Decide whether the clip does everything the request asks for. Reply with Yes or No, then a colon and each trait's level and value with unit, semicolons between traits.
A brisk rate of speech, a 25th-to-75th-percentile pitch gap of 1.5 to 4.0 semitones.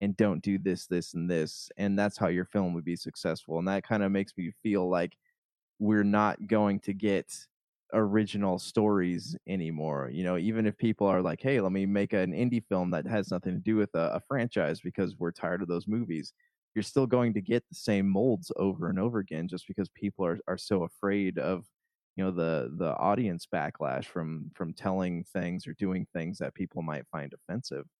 Yes: fast, 210 wpm; average, 2.9 semitones